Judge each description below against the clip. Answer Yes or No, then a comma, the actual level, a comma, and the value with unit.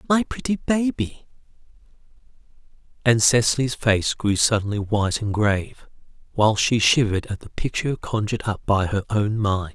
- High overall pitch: No, low, 115 Hz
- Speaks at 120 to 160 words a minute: Yes, average, 140 wpm